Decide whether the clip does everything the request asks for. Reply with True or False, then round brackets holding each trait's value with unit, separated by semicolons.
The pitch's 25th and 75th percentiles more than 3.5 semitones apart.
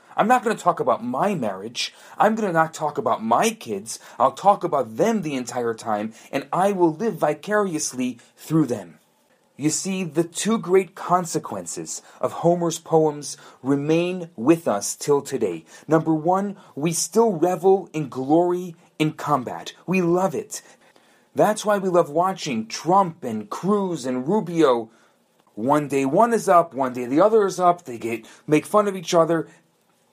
True (4.6 semitones)